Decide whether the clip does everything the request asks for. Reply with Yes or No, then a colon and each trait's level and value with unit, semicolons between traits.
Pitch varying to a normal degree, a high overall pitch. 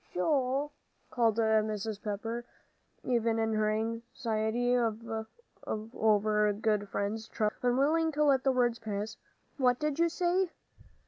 Yes: average, 3.0 semitones; high, 225 Hz